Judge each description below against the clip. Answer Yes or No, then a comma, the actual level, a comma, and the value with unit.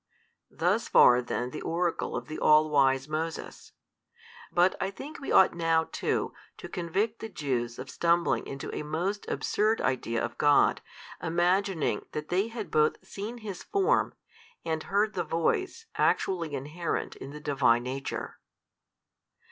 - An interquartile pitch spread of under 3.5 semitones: No, average, 5.3 semitones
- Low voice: No, medium, 165 Hz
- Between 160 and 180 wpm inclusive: No, average, 150 wpm